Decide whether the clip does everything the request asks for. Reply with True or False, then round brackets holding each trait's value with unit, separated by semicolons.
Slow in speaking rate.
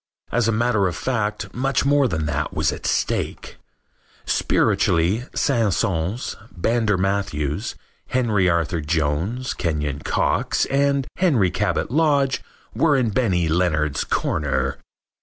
True (120 wpm)